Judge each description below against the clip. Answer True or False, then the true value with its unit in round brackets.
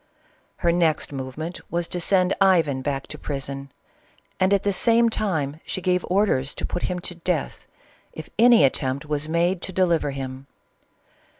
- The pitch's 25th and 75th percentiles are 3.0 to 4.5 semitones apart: False (4.9 semitones)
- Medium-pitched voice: True (170 Hz)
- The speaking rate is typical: True (165 wpm)